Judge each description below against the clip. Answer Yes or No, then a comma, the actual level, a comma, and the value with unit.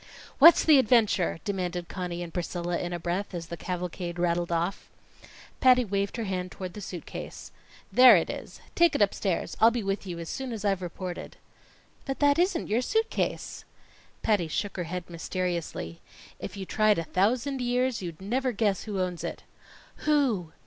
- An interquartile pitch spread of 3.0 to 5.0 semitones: No, wide, 5.4 semitones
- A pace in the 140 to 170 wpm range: No, average, 180 wpm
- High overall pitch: Yes, high, 195 Hz